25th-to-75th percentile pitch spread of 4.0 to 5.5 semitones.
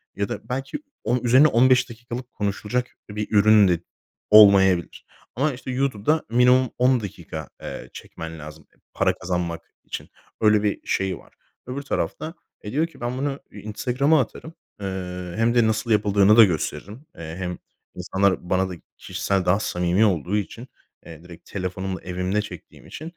Yes: average, 5.2 semitones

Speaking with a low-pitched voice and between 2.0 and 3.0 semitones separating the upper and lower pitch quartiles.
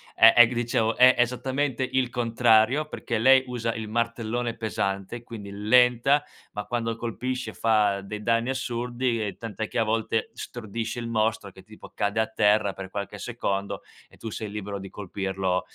Yes: low, 115 Hz; average, 2.7 semitones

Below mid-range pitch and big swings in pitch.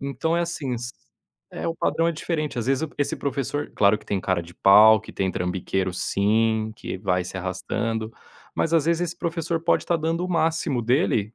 Yes: low, 125 Hz; wide, 8.4 semitones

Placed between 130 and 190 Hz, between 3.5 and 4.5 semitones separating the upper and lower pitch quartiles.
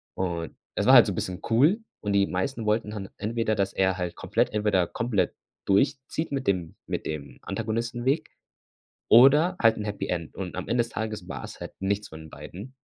No: low, 105 Hz; average, 4.0 semitones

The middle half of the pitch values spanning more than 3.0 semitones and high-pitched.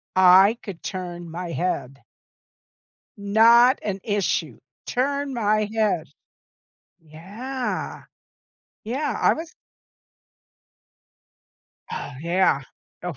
Yes: average, 5.3 semitones; high, 200 Hz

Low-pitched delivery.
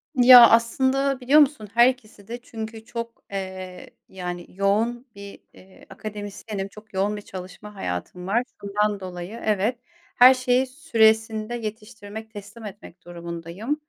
No: high, 215 Hz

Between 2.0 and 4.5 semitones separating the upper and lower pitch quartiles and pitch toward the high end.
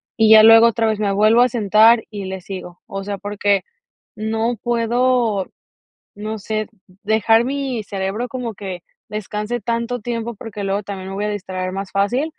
Yes: average, 2.7 semitones; high, 215 Hz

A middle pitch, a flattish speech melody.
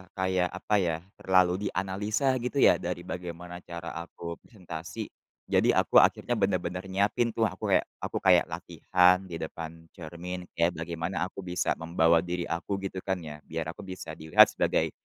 No: very low, 90 Hz; narrow, 2.2 semitones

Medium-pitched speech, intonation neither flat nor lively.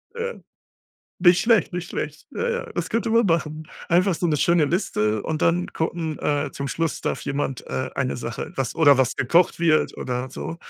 Yes: medium, 160 Hz; average, 4.2 semitones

